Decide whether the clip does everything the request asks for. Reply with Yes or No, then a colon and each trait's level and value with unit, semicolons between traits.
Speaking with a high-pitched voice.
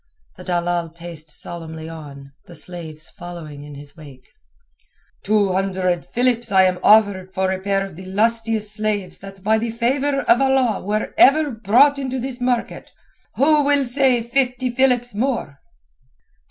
Yes: high, 205 Hz